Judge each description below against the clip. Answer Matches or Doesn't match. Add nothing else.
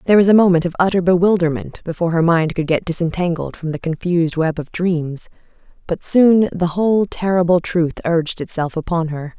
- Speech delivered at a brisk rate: Doesn't match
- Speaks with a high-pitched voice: Doesn't match